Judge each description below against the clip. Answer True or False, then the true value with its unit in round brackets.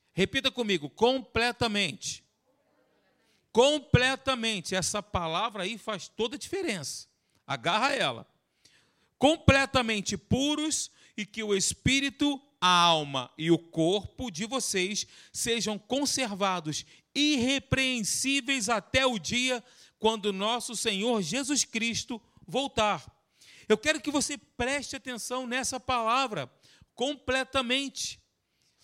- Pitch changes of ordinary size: True (4.3 semitones)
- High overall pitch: True (240 Hz)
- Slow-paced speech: True (100 wpm)